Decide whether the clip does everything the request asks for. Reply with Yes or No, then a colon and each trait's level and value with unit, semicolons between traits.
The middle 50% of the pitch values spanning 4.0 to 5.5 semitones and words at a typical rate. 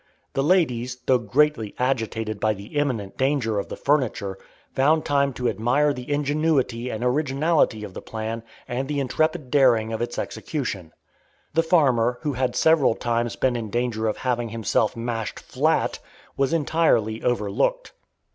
Yes: average, 4.3 semitones; average, 155 wpm